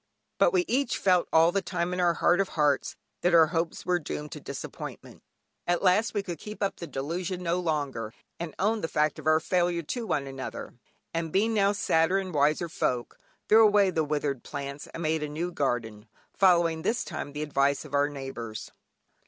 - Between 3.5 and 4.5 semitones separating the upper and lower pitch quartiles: Yes, average, 3.9 semitones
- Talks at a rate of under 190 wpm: No, average, 200 wpm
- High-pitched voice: No, medium, 165 Hz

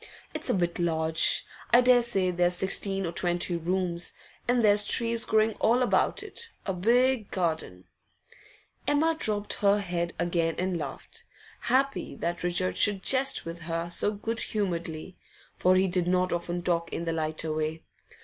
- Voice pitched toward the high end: No, medium, 180 Hz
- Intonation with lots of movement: No, average, 4.1 semitones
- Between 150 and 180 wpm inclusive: Yes, average, 160 wpm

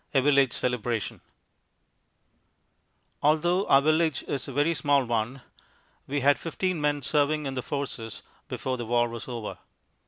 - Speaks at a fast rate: No, average, 145 wpm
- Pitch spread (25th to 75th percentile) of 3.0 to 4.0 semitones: Yes, average, 3.4 semitones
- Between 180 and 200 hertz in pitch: No, medium, 140 Hz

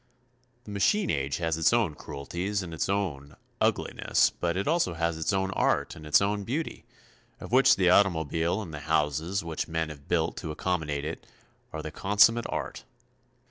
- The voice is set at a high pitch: No, very low, 85 Hz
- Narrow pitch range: No, average, 4.3 semitones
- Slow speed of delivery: No, average, 180 wpm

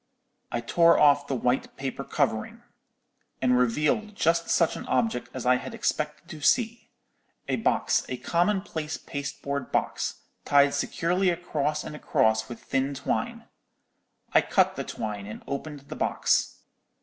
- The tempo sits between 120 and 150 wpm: Yes, average, 145 wpm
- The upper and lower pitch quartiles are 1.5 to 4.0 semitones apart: No, average, 4.7 semitones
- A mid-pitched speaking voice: Yes, medium, 145 Hz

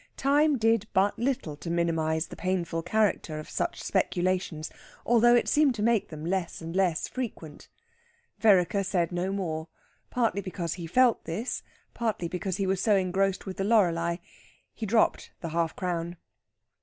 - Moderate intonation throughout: Yes, average, 4.5 semitones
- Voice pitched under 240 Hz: Yes, medium, 185 Hz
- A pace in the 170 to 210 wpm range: No, average, 160 wpm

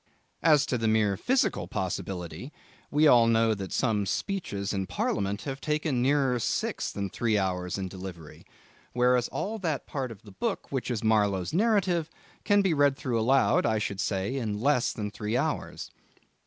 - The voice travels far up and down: Yes, wide, 6.2 semitones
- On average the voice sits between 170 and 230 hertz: No, low, 115 Hz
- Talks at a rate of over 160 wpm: Yes, average, 170 wpm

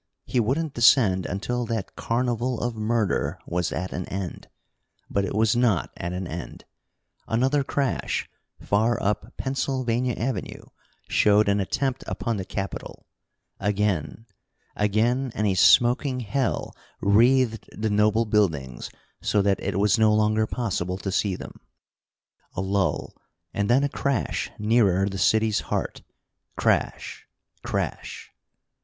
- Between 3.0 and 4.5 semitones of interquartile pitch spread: Yes, average, 3.6 semitones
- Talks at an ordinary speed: No, slow, 130 wpm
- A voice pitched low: Yes, low, 110 Hz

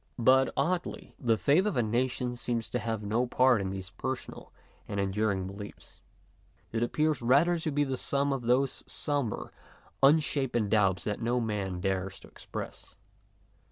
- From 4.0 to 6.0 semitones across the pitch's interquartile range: Yes, average, 4.7 semitones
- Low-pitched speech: Yes, low, 120 Hz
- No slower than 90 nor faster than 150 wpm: No, average, 160 wpm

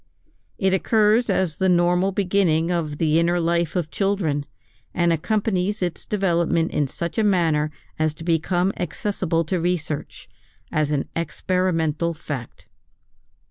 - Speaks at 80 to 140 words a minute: Yes, slow, 135 wpm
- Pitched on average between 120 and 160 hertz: No, medium, 170 Hz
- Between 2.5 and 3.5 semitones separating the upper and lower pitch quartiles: Yes, average, 3.0 semitones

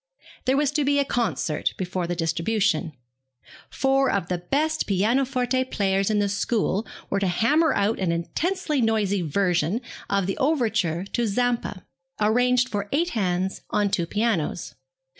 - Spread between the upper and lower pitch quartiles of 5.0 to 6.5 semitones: Yes, average, 5.3 semitones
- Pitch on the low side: No, high, 210 Hz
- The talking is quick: No, average, 150 wpm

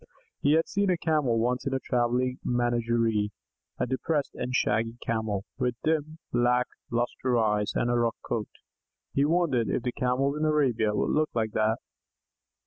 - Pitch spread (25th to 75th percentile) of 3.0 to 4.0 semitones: Yes, average, 3.3 semitones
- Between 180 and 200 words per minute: No, average, 165 wpm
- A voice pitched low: Yes, low, 120 Hz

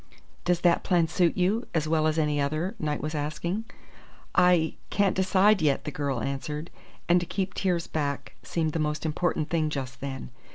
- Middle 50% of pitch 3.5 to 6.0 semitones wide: No, average, 3.1 semitones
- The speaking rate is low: No, average, 180 wpm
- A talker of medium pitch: Yes, medium, 160 Hz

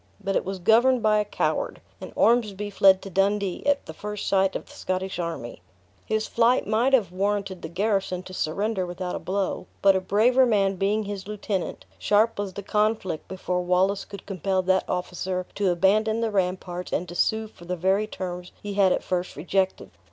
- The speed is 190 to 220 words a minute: Yes, average, 195 wpm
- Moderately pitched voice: No, high, 195 Hz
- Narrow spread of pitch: Yes, narrow, 2.3 semitones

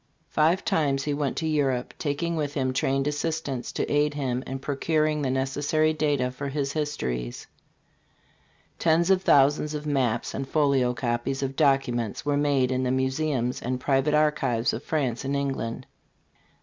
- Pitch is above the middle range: No, medium, 140 Hz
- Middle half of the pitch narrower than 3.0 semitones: Yes, narrow, 2.5 semitones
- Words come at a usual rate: Yes, average, 160 wpm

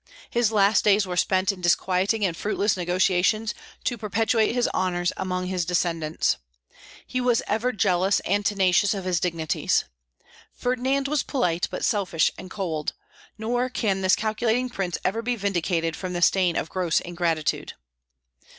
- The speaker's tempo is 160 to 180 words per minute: No, average, 150 wpm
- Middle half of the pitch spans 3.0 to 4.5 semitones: Yes, average, 3.7 semitones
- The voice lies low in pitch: No, high, 190 Hz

